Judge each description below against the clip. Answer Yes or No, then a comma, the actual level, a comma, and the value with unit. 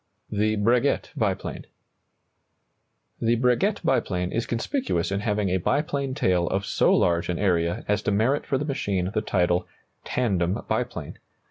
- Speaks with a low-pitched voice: Yes, low, 105 Hz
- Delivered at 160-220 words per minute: No, average, 145 wpm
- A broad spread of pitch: Yes, wide, 5.7 semitones